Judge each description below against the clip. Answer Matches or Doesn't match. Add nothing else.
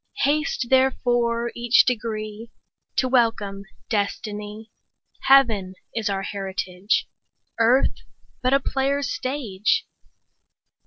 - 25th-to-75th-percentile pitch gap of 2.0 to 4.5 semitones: Matches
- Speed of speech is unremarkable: Doesn't match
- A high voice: Matches